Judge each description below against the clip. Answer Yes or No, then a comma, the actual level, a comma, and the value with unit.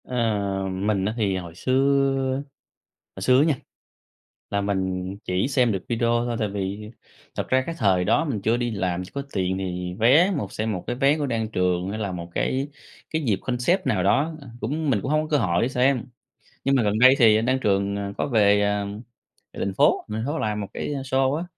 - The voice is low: Yes, low, 110 Hz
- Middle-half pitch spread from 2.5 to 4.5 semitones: No, average, 5.1 semitones